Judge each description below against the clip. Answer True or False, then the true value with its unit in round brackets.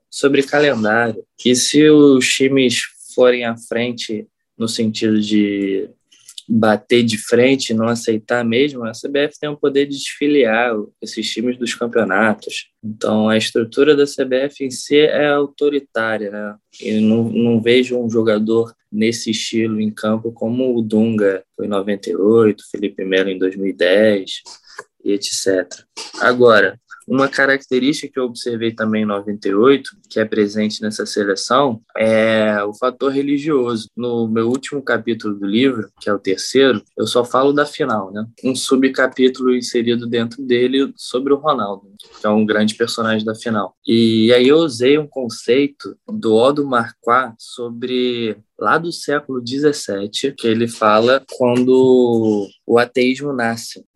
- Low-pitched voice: True (115 Hz)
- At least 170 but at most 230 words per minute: False (145 wpm)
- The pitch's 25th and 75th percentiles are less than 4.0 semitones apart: True (3.4 semitones)